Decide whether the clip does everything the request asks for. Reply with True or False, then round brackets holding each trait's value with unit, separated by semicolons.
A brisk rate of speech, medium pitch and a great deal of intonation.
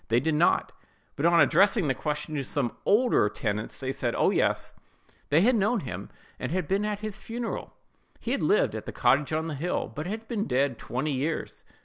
True (210 wpm; 160 Hz; 7.5 semitones)